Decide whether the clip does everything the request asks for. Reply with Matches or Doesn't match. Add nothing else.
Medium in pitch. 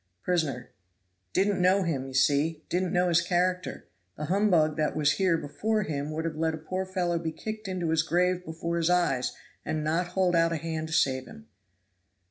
Matches